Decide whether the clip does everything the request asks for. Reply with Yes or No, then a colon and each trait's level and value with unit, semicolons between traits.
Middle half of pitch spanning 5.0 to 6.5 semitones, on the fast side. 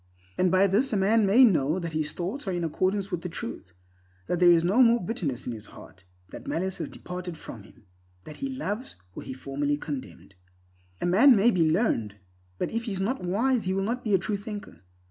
Yes: wide, 5.6 semitones; fast, 220 wpm